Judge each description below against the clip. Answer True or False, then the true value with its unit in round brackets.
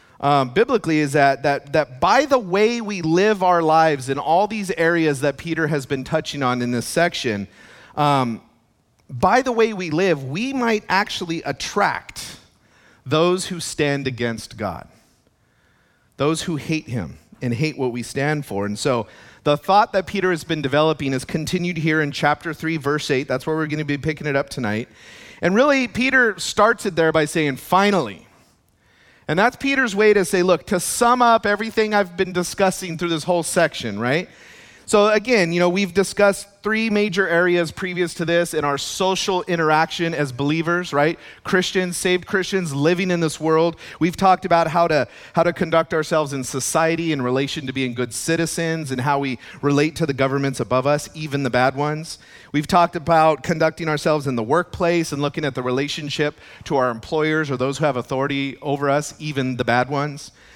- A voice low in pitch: False (160 Hz)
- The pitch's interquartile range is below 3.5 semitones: False (4.3 semitones)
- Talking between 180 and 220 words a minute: True (185 wpm)